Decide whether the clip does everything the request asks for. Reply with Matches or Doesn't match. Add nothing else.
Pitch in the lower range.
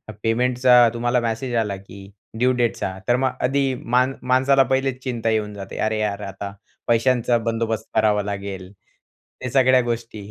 Matches